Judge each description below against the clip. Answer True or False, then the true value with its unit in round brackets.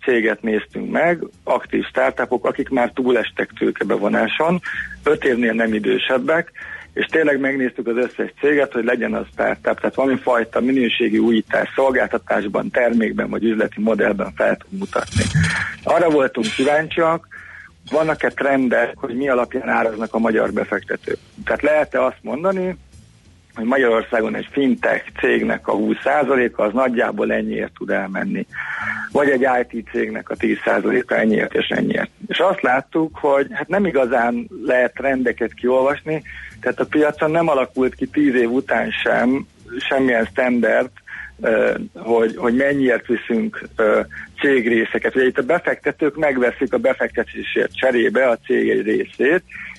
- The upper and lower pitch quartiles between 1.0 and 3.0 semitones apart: False (4.1 semitones)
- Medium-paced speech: True (135 wpm)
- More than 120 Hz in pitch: True (130 Hz)